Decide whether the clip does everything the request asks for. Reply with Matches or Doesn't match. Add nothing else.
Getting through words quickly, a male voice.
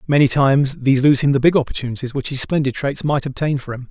Matches